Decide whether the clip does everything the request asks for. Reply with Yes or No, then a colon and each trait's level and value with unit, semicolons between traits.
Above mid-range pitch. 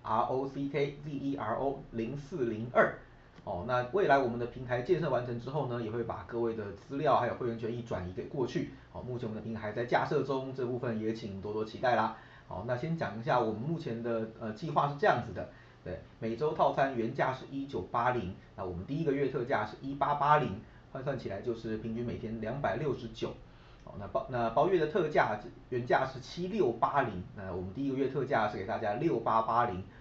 No: low, 120 Hz